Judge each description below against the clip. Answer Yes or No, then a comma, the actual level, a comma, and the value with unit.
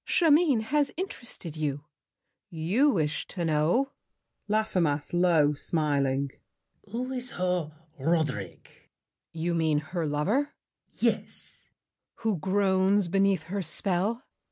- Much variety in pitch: Yes, wide, 6.0 semitones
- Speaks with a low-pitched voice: No, medium, 180 Hz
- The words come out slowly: Yes, slow, 115 wpm